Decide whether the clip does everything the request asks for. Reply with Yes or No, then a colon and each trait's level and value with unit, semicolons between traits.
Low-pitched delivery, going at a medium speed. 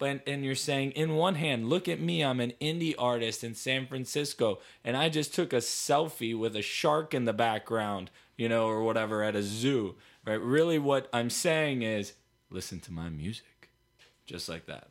Yes: low, 125 Hz; average, 195 wpm